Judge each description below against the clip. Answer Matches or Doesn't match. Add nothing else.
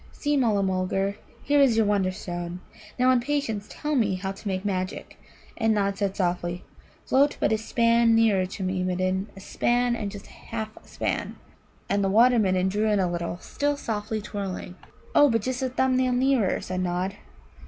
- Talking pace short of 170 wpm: Doesn't match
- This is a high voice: Matches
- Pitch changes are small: Doesn't match